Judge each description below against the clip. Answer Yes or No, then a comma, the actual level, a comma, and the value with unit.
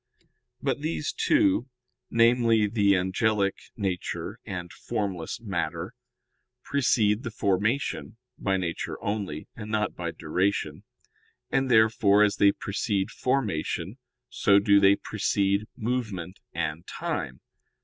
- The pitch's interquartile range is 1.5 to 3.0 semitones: Yes, average, 2.7 semitones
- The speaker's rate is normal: No, slow, 110 wpm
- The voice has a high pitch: No, low, 100 Hz